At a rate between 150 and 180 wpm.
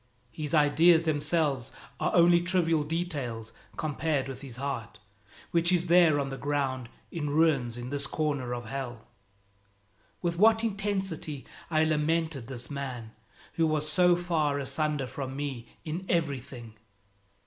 No: slow, 135 wpm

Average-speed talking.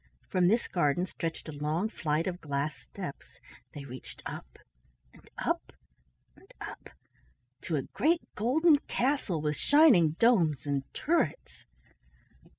No: slow, 130 wpm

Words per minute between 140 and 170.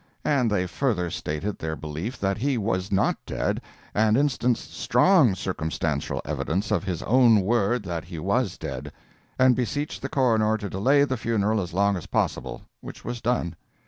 Yes: average, 165 wpm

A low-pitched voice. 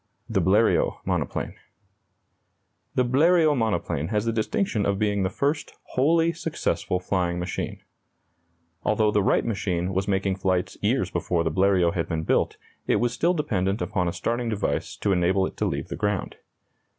Yes: low, 100 Hz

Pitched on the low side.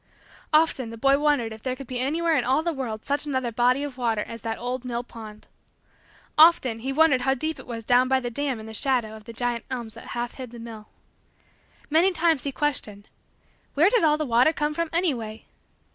No: very high, 255 Hz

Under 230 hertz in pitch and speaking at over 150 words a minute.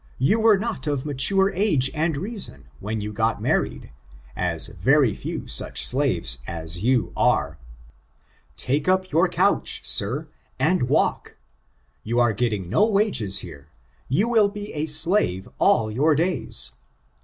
No: medium, 140 Hz; average, 145 wpm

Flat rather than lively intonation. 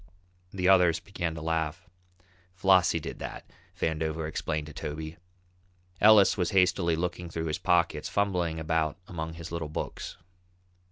Yes: narrow, 2.2 semitones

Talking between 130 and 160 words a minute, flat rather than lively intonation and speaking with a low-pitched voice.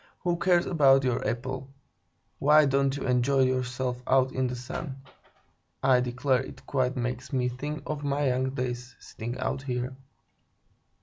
Yes: average, 150 wpm; narrow, 1.7 semitones; low, 130 Hz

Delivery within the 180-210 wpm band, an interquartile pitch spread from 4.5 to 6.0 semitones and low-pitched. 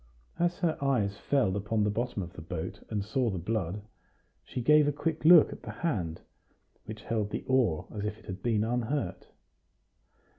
Yes: average, 185 wpm; wide, 5.4 semitones; low, 110 Hz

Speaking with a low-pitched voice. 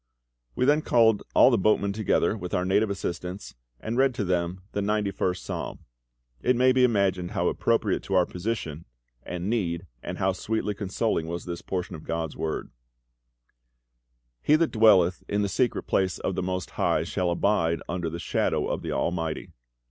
Yes: very low, 95 Hz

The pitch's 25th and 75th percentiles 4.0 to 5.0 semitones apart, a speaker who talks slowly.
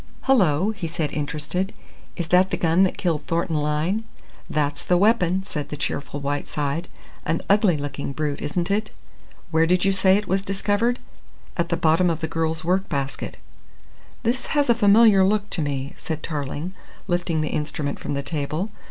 No: average, 4.5 semitones; average, 175 wpm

